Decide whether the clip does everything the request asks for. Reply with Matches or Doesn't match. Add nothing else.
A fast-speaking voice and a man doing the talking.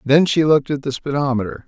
Matches